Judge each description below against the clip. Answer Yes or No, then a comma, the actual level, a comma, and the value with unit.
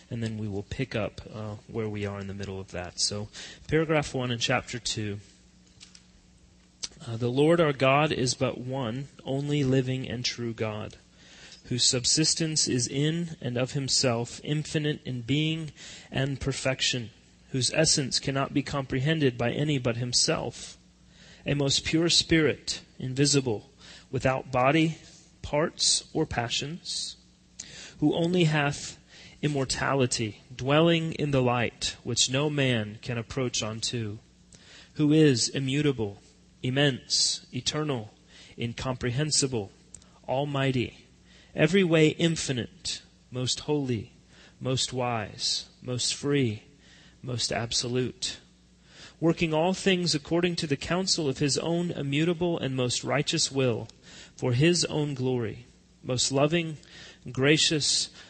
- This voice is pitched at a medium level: No, low, 130 Hz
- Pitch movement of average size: Yes, average, 4.1 semitones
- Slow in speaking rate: Yes, slow, 120 wpm